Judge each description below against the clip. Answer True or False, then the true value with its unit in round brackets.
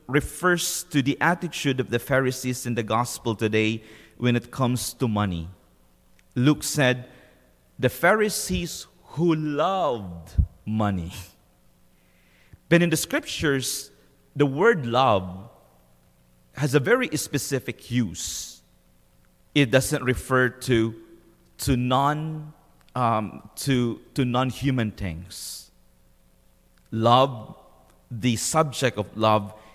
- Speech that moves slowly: True (105 wpm)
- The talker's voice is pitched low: True (125 Hz)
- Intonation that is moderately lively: False (6.1 semitones)